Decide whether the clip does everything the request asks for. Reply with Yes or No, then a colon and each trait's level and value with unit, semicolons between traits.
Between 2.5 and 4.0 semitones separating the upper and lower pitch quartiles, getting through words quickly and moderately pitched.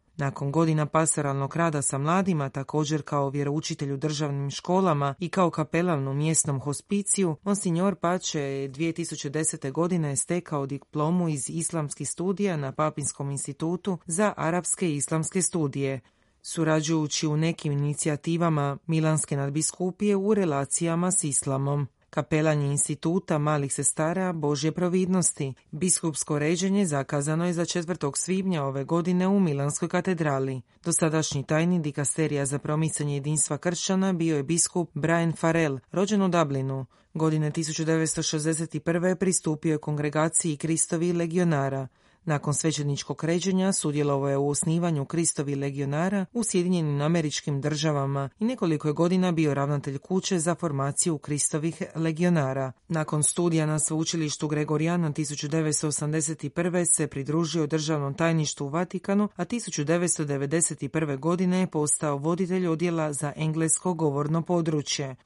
No: average, 3.0 semitones; average, 120 wpm; medium, 160 Hz